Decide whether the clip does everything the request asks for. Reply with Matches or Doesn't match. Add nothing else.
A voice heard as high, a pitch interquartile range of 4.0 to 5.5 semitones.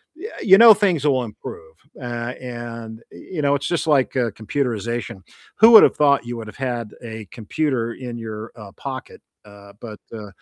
Doesn't match